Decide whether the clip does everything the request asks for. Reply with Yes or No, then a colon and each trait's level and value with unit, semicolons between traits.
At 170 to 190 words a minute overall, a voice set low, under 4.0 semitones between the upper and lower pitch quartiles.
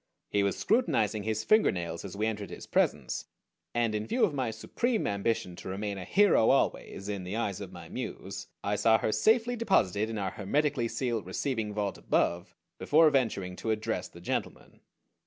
No: average, 180 wpm; low, 110 Hz; average, 5.3 semitones